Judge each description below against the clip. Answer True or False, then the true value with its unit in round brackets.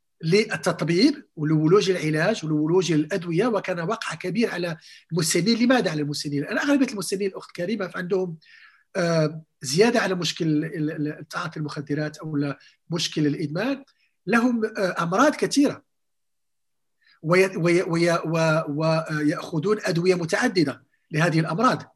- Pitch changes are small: False (4.1 semitones)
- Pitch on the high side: False (175 Hz)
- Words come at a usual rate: True (95 wpm)